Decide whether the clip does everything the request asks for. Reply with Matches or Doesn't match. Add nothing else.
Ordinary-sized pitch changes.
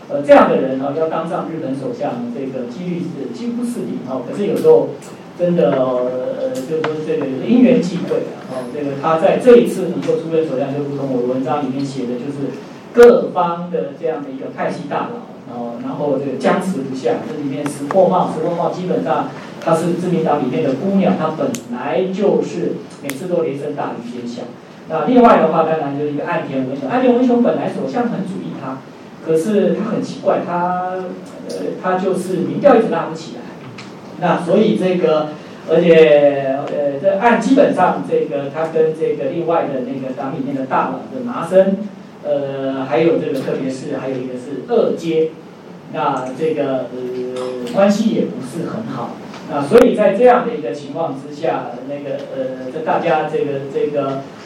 Doesn't match